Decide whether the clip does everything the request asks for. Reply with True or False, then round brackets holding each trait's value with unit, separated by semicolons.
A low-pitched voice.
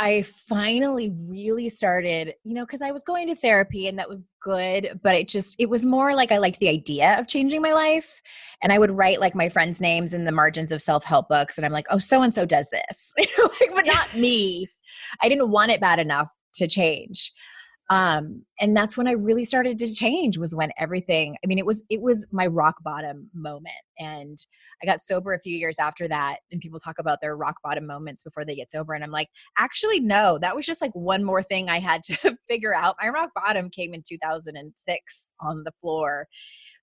False (190 Hz)